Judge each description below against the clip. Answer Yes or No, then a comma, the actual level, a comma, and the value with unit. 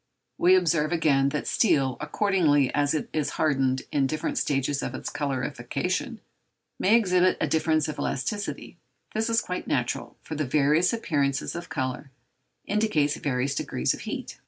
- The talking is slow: No, average, 155 wpm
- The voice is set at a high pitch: No, medium, 150 Hz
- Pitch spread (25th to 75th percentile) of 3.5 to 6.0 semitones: Yes, average, 4.7 semitones